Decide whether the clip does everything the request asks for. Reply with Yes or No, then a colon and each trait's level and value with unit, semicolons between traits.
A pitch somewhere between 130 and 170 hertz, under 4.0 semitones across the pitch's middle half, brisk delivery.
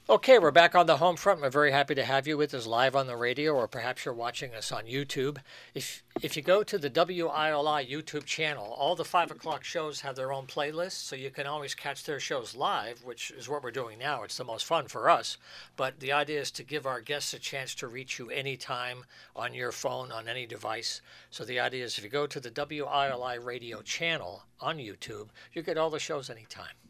Yes: medium, 140 Hz; average, 2.7 semitones; fast, 230 wpm